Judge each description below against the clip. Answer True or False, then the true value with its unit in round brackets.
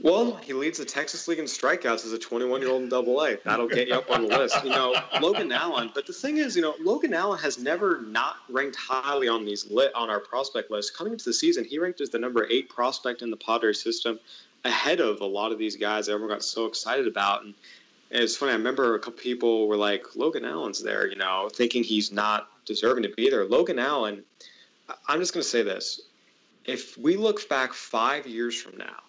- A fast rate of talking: True (230 wpm)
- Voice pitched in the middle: False (120 Hz)